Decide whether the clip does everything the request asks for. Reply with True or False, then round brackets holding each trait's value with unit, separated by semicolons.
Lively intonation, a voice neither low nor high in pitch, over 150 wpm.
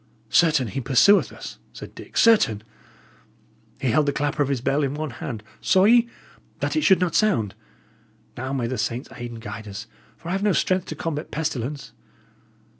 True (6.8 semitones; 145 Hz; 190 wpm)